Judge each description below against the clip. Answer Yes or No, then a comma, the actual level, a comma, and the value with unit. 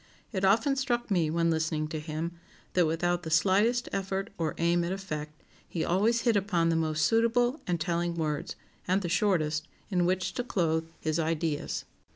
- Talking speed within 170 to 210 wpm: Yes, average, 180 wpm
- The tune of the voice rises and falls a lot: No, average, 3.6 semitones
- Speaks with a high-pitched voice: No, medium, 175 Hz